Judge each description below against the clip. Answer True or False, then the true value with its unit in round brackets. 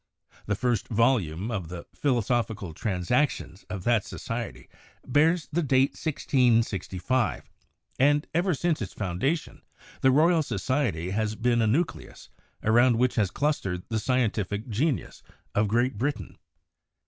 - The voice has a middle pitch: False (120 Hz)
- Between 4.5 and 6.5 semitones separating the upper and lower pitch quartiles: True (4.9 semitones)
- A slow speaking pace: True (125 wpm)